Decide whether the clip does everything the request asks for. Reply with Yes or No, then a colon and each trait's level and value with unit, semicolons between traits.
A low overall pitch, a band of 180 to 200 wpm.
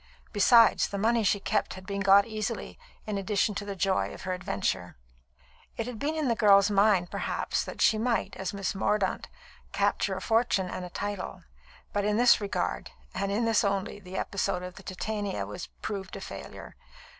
No: high, 200 Hz; average, 185 wpm